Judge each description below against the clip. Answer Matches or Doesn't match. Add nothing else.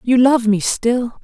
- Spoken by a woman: Matches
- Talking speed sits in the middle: Matches